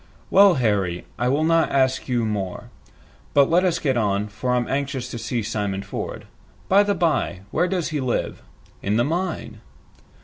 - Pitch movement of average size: No, wide, 7.3 semitones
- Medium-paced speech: Yes, average, 175 wpm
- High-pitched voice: No, low, 130 Hz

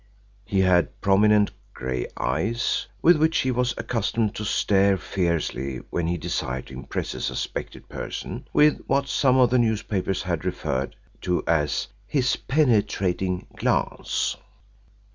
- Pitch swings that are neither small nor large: No, wide, 6.0 semitones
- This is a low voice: Yes, low, 100 Hz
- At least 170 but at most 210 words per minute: No, slow, 135 wpm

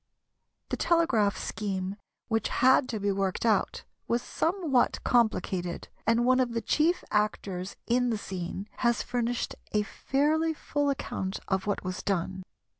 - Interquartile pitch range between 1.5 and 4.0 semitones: No, average, 4.7 semitones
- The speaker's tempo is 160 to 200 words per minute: No, average, 145 wpm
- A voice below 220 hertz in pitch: No, high, 225 Hz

